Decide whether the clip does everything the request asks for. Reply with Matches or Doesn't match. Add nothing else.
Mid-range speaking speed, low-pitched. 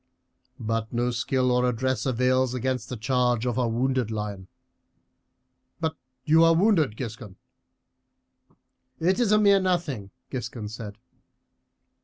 Doesn't match